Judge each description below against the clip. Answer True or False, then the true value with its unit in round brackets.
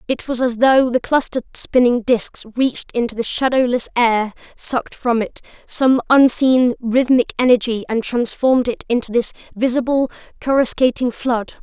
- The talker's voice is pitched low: False (245 Hz)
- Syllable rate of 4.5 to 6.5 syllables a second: True (4.9 syllables/s)